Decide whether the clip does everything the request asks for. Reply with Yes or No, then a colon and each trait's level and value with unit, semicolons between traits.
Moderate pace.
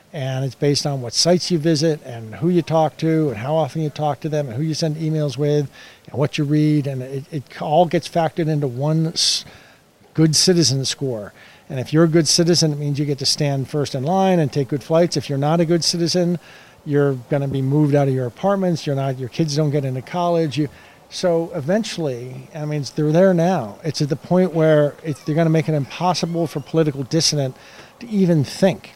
No: fast, 225 wpm